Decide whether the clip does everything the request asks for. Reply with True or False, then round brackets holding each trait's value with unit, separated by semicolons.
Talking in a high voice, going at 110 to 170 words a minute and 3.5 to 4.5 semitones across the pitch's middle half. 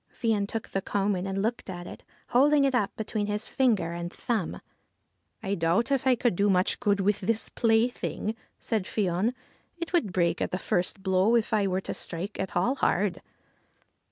False (205 Hz; 190 wpm; 3.8 semitones)